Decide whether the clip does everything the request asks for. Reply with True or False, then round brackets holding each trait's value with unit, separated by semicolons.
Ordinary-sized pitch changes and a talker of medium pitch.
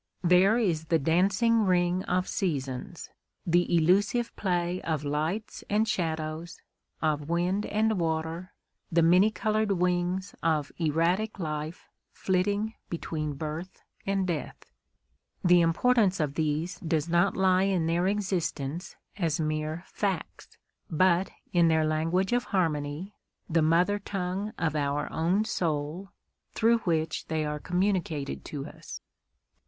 True (3.4 semitones; 175 Hz)